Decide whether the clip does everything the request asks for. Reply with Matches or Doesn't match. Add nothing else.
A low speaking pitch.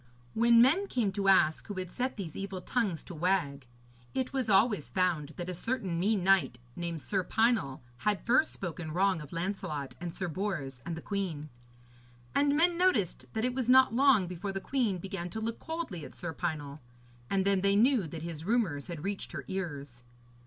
Doesn't match